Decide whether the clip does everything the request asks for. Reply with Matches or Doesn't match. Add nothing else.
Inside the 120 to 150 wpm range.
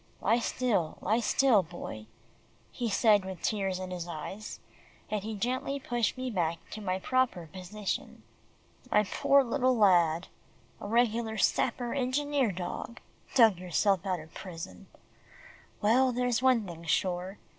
Matches